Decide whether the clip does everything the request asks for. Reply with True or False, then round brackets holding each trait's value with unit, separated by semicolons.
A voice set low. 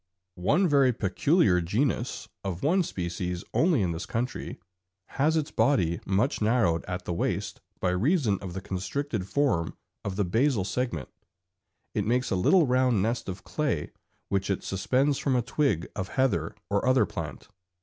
True (105 Hz)